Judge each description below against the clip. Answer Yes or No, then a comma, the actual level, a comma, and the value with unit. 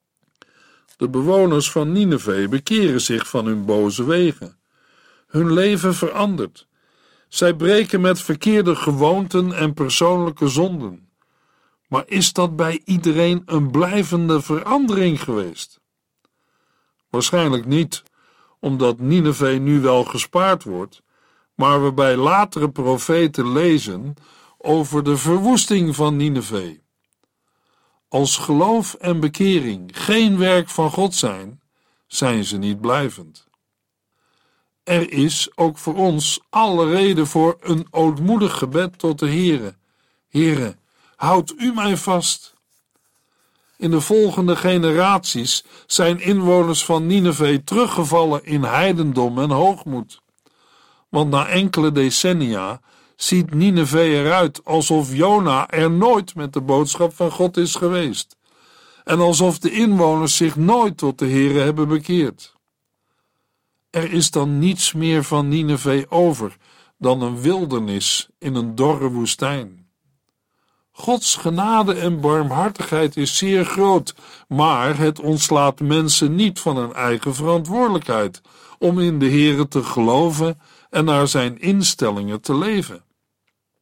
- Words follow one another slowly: Yes, slow, 120 wpm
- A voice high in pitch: No, medium, 160 Hz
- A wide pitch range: No, average, 4.6 semitones